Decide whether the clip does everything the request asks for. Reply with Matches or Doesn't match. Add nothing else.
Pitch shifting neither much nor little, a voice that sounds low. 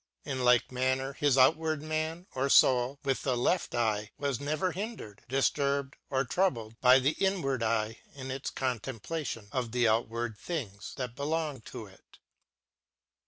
Matches